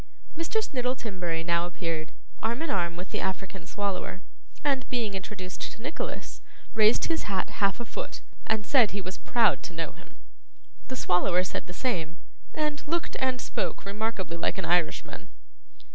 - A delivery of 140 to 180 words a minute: Yes, average, 165 wpm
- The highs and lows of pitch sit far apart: Yes, wide, 5.8 semitones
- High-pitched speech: Yes, high, 200 Hz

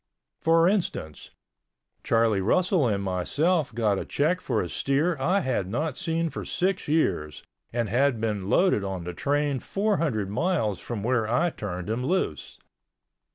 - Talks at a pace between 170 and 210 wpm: No, average, 155 wpm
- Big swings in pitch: Yes, wide, 8.3 semitones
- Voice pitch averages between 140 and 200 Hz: No, low, 125 Hz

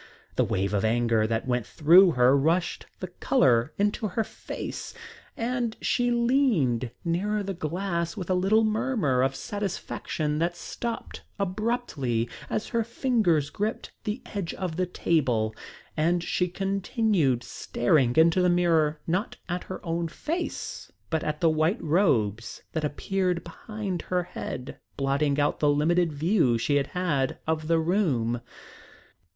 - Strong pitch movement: Yes, wide, 5.8 semitones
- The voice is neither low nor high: Yes, medium, 170 Hz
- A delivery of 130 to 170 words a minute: Yes, average, 145 wpm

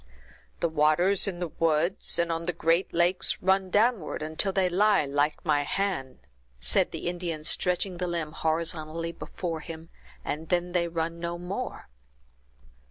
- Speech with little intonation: Yes, narrow, 2.3 semitones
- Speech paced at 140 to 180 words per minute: Yes, average, 155 wpm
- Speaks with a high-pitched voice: No, medium, 170 Hz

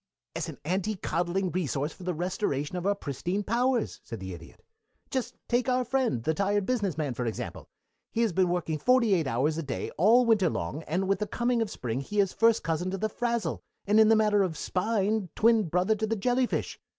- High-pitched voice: Yes, high, 195 Hz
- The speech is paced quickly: Yes, fast, 220 wpm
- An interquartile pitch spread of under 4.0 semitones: No, wide, 5.5 semitones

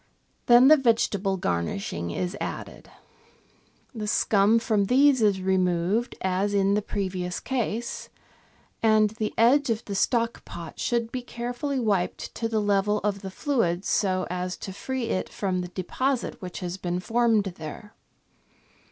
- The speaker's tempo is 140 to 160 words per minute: Yes, average, 150 wpm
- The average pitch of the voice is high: Yes, high, 205 Hz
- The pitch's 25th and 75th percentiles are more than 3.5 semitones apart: Yes, average, 4.1 semitones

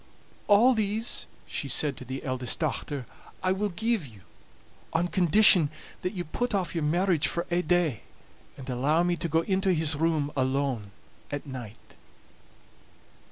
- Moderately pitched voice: Yes, medium, 165 Hz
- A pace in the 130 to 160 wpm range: Yes, average, 155 wpm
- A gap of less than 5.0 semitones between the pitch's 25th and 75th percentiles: No, average, 5.3 semitones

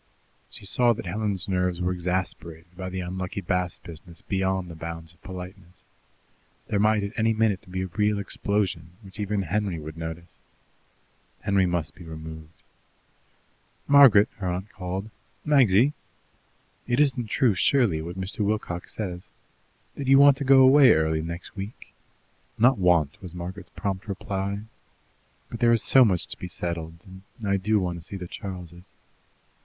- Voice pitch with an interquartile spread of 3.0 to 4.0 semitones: Yes, average, 3.4 semitones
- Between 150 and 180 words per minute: Yes, average, 160 wpm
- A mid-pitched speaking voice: No, very low, 95 Hz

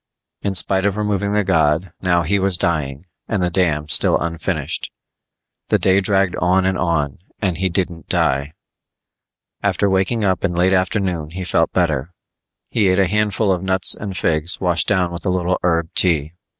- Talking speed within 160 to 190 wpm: Yes, average, 175 wpm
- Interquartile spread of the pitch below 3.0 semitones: Yes, narrow, 2.6 semitones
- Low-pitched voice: Yes, very low, 90 Hz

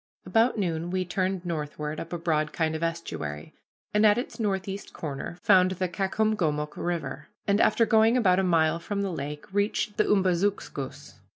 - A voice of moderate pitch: Yes, medium, 180 Hz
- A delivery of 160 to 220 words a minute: Yes, average, 170 wpm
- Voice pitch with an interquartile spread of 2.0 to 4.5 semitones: Yes, average, 4.2 semitones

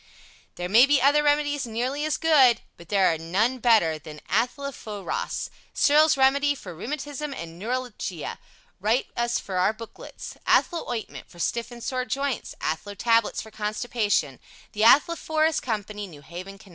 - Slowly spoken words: No, average, 165 wpm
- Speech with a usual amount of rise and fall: No, wide, 6.0 semitones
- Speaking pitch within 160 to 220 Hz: No, high, 235 Hz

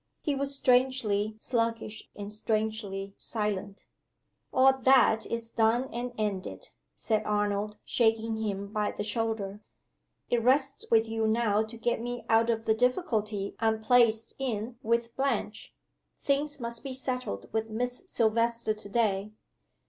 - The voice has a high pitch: Yes, high, 225 Hz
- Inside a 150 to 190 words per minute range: No, average, 140 wpm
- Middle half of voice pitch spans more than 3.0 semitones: No, narrow, 2.4 semitones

